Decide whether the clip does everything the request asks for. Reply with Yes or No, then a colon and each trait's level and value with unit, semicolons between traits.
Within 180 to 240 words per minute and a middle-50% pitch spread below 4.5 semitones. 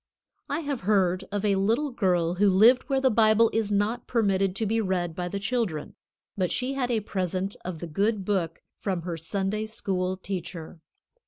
Yes: average, 185 wpm; average, 3.4 semitones